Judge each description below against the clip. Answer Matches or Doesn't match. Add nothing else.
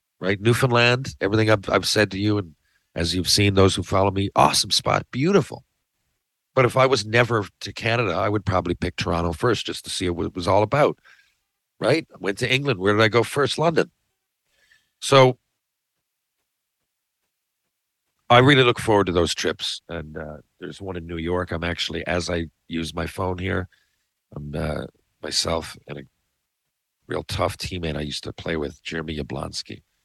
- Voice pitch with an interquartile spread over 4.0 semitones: Matches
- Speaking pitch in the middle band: Doesn't match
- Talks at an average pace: Matches